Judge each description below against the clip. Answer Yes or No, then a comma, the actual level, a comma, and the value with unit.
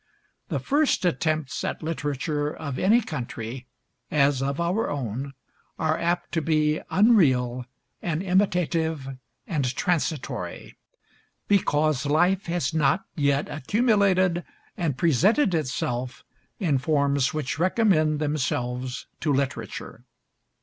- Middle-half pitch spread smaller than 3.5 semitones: No, average, 4.2 semitones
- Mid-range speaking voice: Yes, medium, 155 Hz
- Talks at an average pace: No, slow, 110 wpm